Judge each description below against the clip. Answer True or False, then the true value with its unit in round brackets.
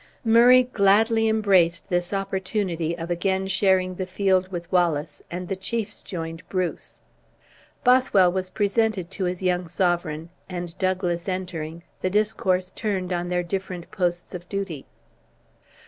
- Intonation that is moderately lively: False (2.2 semitones)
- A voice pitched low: False (185 Hz)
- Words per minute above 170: False (135 wpm)